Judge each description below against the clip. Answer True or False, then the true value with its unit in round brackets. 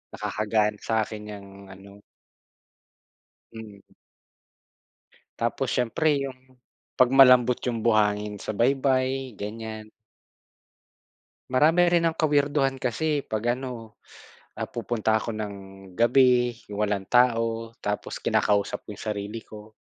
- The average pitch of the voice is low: True (115 Hz)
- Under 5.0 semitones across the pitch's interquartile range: True (3.5 semitones)